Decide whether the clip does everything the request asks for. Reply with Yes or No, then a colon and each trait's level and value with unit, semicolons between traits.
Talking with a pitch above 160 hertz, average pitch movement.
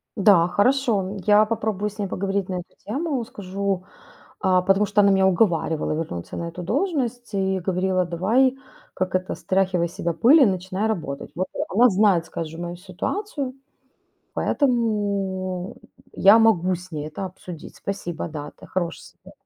Yes: high, 190 Hz; average, 3.2 semitones